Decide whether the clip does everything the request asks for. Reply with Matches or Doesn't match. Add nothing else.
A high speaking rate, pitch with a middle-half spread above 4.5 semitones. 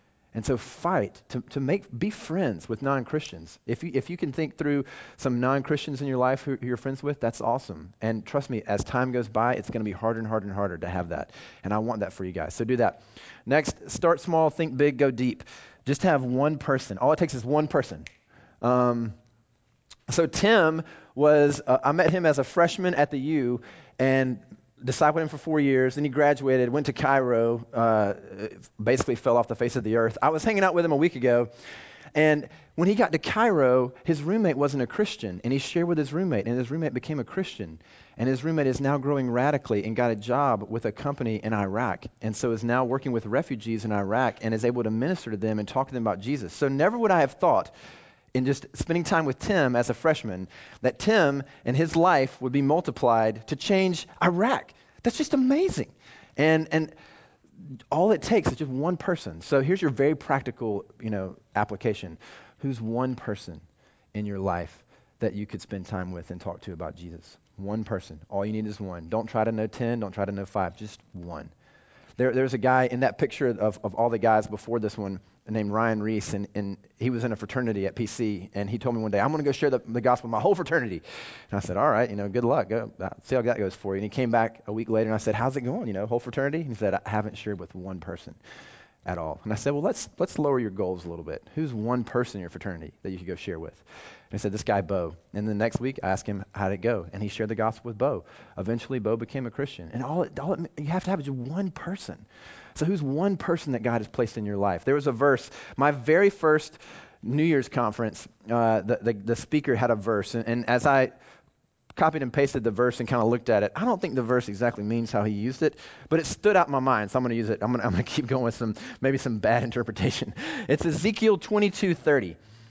Matches